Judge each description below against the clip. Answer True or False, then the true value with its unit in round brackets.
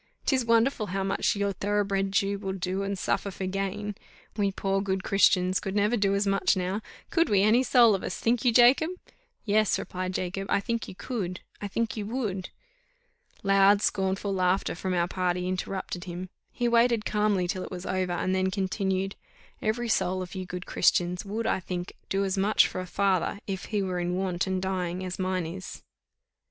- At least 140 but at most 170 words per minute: False (195 wpm)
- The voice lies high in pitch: True (195 Hz)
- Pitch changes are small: True (1.9 semitones)